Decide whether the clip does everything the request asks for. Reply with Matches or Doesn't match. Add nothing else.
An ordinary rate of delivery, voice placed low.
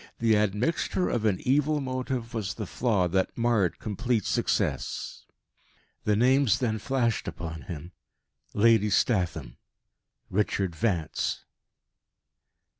Doesn't match